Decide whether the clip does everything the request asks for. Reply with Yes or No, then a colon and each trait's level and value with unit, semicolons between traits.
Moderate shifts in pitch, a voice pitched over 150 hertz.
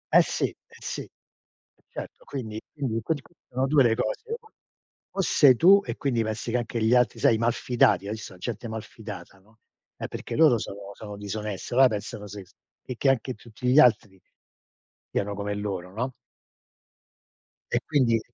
No: average, 3.9 semitones; low, 115 Hz